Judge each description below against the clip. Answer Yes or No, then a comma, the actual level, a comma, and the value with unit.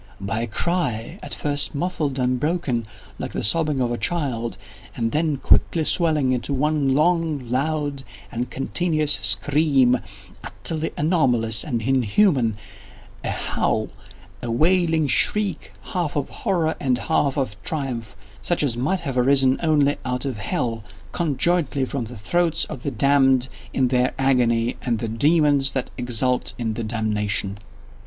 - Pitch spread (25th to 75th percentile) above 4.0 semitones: Yes, average, 4.6 semitones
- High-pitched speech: No, low, 135 Hz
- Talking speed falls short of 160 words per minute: Yes, average, 145 wpm